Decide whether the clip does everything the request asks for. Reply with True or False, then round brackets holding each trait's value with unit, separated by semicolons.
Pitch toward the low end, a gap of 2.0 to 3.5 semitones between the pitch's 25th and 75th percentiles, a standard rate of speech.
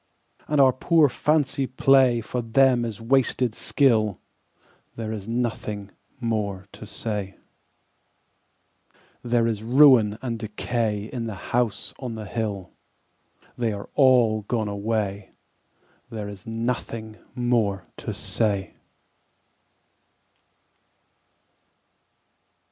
False (115 Hz; 2.8 semitones; 100 wpm)